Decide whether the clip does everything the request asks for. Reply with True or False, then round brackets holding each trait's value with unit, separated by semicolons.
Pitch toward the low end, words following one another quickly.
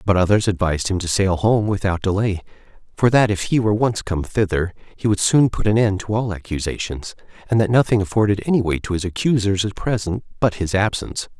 True (100 Hz; 210 wpm)